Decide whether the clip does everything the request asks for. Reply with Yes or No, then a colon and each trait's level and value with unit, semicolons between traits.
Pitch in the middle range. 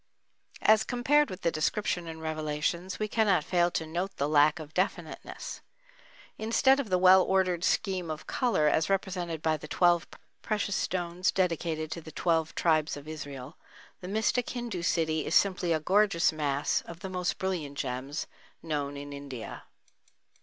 Yes: medium, 170 Hz